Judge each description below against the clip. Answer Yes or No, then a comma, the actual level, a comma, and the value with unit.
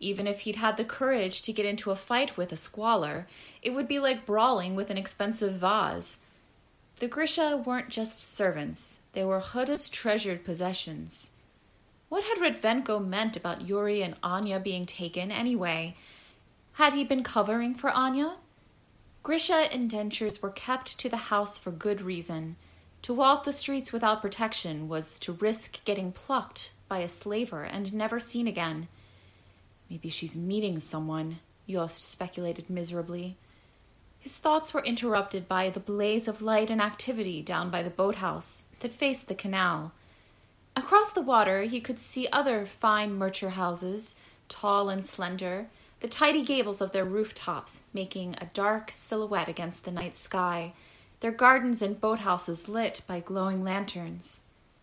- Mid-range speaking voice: No, high, 200 Hz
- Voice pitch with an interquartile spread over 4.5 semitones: Yes, average, 4.9 semitones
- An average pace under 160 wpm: Yes, average, 150 wpm